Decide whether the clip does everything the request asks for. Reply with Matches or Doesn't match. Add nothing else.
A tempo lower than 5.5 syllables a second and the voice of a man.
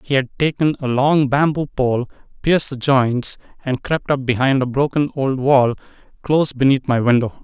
Matches